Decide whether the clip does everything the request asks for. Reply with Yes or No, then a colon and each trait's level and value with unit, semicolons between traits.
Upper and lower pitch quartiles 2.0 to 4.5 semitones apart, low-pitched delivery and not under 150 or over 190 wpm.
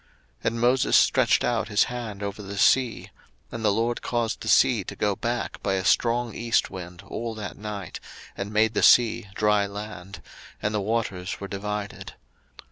Yes: narrow, 2.5 semitones; low, 105 Hz; average, 180 wpm